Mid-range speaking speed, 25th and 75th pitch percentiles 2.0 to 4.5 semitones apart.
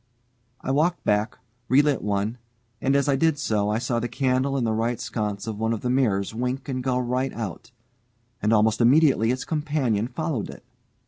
Yes: average, 190 wpm; average, 3.6 semitones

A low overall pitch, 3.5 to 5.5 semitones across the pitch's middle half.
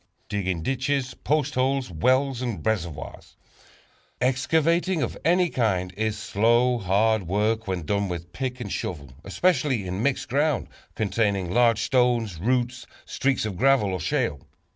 Yes: low, 115 Hz; average, 5.2 semitones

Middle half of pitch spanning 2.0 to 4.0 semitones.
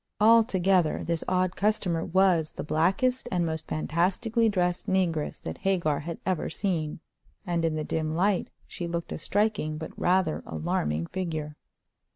Yes: average, 3.3 semitones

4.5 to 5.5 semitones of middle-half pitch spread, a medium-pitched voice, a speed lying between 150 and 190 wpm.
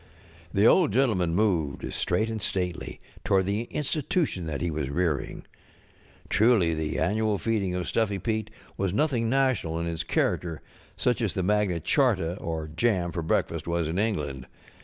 No: average, 5.0 semitones; very low, 95 Hz; average, 160 wpm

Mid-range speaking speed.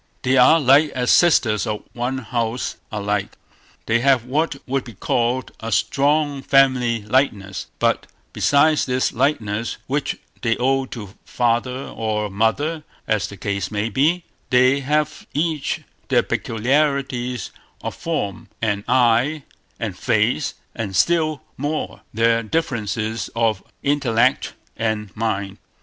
No: slow, 130 wpm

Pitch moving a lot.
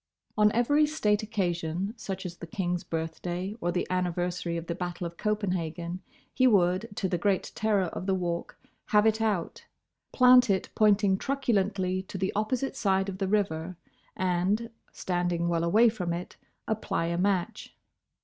No: average, 3.3 semitones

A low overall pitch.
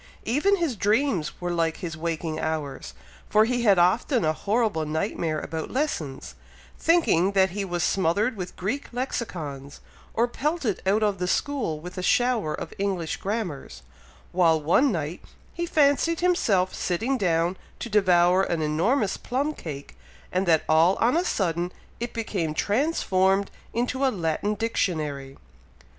No: high, 190 Hz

